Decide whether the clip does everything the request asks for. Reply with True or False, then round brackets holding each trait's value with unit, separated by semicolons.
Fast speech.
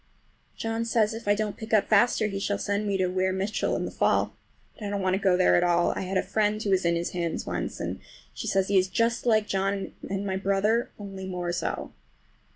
True (245 wpm)